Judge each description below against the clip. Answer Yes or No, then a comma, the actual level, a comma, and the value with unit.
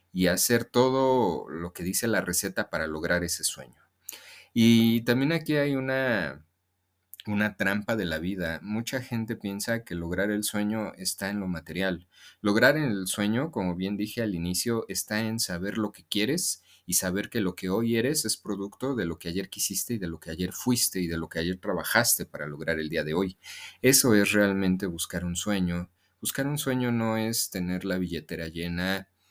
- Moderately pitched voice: No, very low, 95 Hz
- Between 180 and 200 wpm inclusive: Yes, fast, 190 wpm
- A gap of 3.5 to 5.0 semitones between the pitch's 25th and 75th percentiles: Yes, average, 4.1 semitones